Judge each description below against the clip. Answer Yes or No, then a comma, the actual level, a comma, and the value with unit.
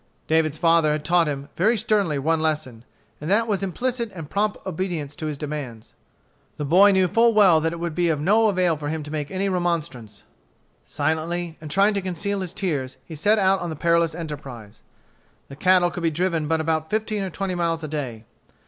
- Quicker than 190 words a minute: Yes, fast, 205 wpm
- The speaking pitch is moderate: Yes, medium, 165 Hz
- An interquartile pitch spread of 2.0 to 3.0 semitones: No, average, 3.8 semitones